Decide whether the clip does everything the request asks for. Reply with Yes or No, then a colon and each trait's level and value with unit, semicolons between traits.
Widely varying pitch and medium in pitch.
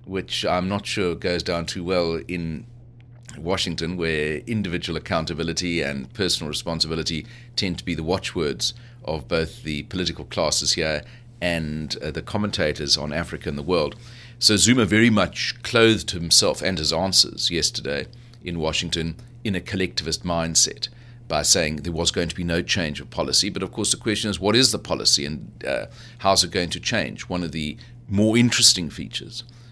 No: wide, 6.2 semitones; very low, 95 Hz